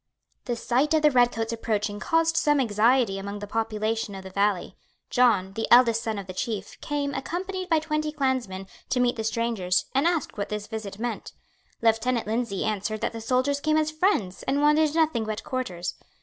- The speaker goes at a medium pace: Yes, average, 190 wpm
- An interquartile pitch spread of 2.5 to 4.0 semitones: No, average, 5.3 semitones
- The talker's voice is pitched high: Yes, high, 230 Hz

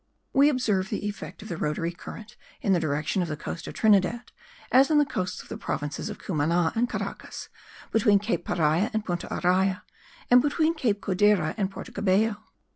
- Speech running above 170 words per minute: Yes, average, 190 wpm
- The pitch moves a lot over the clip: No, average, 4.5 semitones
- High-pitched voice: Yes, high, 195 Hz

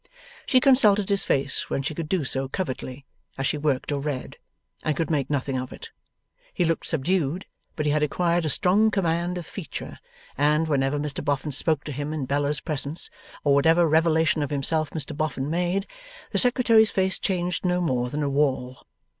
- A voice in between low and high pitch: Yes, medium, 155 Hz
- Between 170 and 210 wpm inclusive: Yes, average, 190 wpm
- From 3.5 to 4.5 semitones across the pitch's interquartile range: Yes, average, 3.8 semitones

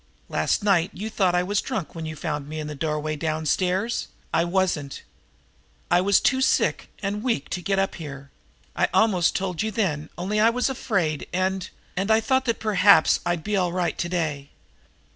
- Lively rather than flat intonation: No, average, 4.6 semitones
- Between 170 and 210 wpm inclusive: Yes, average, 190 wpm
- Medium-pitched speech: Yes, medium, 180 Hz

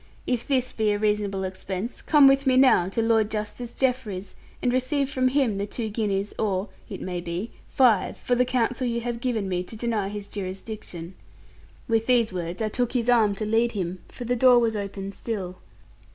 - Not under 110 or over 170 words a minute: No, average, 195 wpm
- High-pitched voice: Yes, high, 220 Hz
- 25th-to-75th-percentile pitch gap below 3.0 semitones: No, average, 3.8 semitones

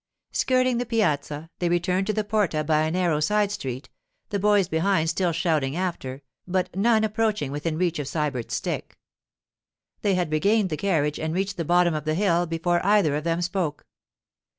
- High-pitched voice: No, medium, 175 Hz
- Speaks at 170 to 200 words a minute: Yes, average, 180 wpm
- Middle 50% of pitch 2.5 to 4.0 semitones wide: No, average, 4.4 semitones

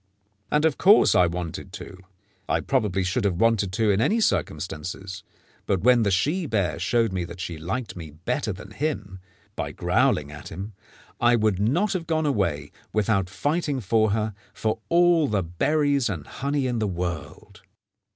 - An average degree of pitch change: No, wide, 7.0 semitones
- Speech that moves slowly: No, average, 170 wpm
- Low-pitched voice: Yes, low, 105 Hz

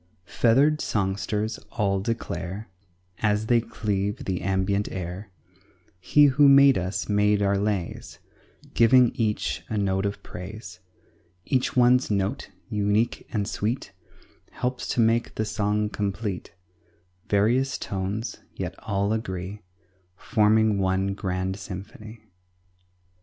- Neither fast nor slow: No, slow, 115 wpm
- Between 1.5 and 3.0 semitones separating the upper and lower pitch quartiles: Yes, average, 2.7 semitones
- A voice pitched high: No, low, 105 Hz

